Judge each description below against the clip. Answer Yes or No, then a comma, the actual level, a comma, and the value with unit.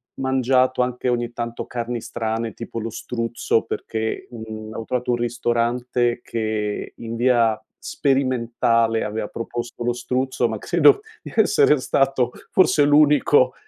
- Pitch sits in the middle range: No, low, 120 Hz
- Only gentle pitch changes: Yes, narrow, 1.8 semitones